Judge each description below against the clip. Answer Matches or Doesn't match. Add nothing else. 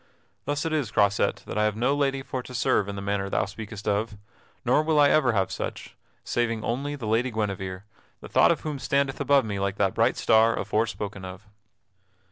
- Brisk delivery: Matches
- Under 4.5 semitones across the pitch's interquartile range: Doesn't match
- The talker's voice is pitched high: Doesn't match